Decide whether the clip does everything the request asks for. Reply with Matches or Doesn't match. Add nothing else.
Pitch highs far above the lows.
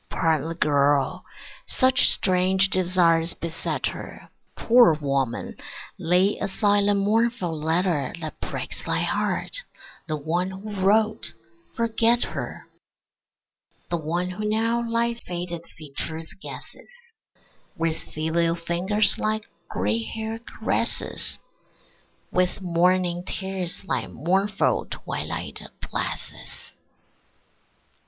Doesn't match